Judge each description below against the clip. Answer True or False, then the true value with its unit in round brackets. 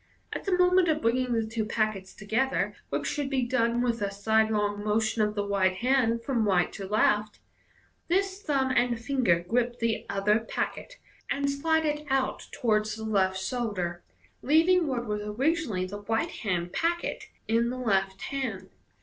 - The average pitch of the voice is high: True (230 Hz)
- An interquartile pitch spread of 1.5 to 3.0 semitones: False (4.5 semitones)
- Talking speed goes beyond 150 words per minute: True (165 wpm)